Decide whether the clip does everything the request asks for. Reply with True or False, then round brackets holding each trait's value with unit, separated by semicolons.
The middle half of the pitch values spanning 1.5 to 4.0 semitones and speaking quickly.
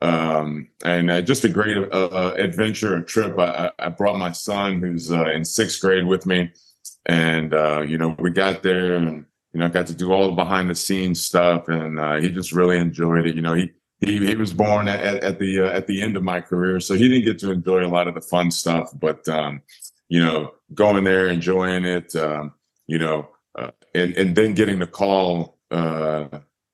True (2.5 semitones; 220 wpm)